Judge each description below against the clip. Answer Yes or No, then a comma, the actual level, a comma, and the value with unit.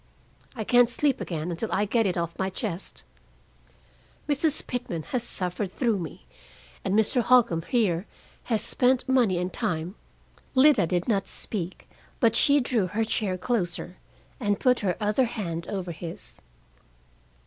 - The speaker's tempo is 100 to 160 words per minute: Yes, average, 150 wpm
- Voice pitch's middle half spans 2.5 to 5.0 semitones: No, wide, 5.5 semitones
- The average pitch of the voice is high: Yes, high, 205 Hz